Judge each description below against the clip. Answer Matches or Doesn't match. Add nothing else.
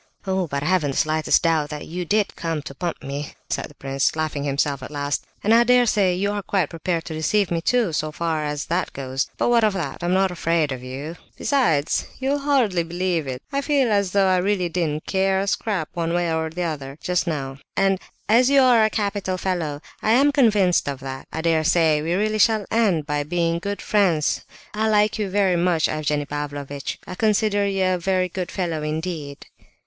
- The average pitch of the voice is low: Doesn't match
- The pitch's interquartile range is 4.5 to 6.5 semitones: Matches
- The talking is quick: Matches